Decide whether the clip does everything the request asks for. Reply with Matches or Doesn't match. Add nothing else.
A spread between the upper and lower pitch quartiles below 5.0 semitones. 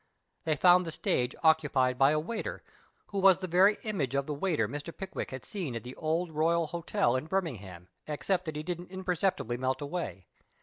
Doesn't match